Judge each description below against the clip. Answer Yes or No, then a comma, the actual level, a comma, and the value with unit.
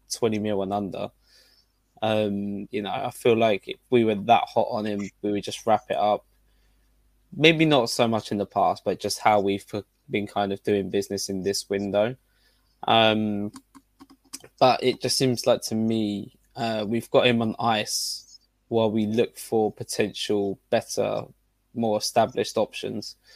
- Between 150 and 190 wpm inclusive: Yes, average, 165 wpm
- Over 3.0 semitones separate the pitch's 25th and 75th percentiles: No, narrow, 2.5 semitones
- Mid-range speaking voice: No, low, 110 Hz